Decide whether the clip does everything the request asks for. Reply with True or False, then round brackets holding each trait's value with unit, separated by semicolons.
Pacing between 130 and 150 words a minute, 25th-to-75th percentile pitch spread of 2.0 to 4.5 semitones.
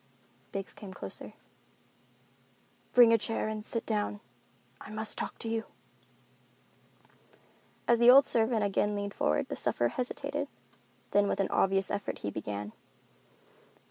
True (135 wpm; 2.6 semitones)